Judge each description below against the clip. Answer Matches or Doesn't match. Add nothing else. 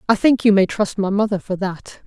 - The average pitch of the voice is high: Matches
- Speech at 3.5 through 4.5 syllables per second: Doesn't match